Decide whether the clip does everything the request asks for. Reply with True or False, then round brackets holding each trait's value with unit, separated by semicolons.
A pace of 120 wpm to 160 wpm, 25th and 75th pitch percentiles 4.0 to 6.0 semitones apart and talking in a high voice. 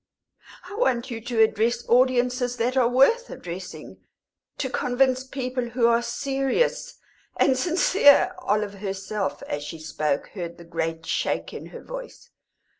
True (140 wpm; 5.0 semitones; 245 Hz)